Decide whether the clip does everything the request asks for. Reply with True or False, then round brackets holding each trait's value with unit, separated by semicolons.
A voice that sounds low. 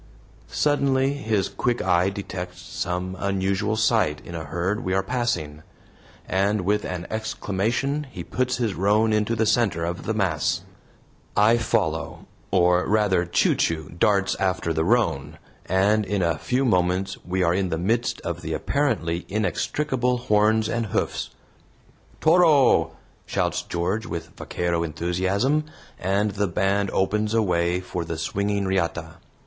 True (95 Hz)